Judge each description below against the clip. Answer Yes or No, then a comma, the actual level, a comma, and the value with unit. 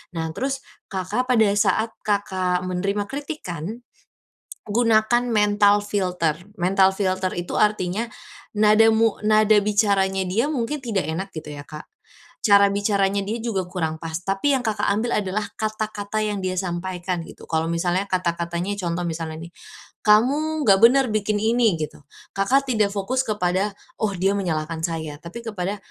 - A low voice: No, high, 200 Hz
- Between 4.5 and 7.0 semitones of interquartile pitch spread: No, average, 3.4 semitones